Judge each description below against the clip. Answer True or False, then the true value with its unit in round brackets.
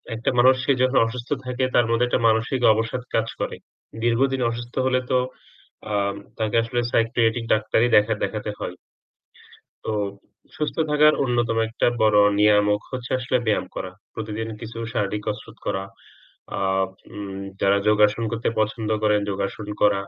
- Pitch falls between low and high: False (115 Hz)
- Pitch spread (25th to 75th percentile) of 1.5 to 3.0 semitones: True (2.5 semitones)